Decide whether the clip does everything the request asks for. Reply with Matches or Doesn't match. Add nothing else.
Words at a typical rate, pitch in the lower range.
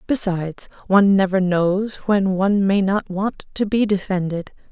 Doesn't match